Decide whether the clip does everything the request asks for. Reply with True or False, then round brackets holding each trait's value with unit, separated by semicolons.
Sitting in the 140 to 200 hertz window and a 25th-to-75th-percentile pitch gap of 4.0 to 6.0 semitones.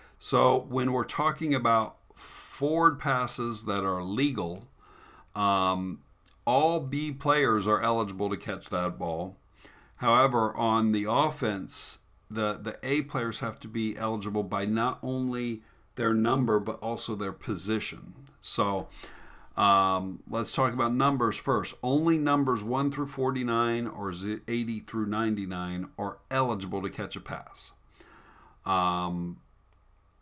False (110 Hz; 4.5 semitones)